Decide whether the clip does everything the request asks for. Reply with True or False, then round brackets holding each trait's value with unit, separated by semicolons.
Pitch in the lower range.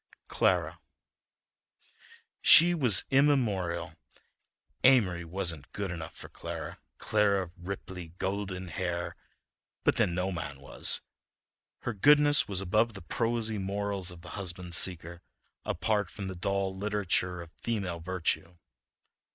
True (95 Hz)